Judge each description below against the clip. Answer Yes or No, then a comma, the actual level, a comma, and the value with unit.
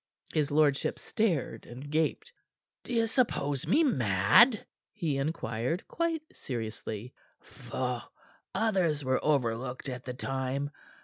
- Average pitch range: No, wide, 7.1 semitones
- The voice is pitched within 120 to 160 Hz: Yes, medium, 140 Hz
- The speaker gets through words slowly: Yes, slow, 115 wpm